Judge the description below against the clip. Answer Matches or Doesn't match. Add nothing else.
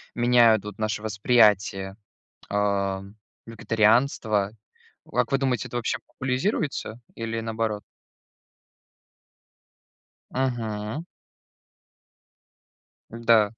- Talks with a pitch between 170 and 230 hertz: Doesn't match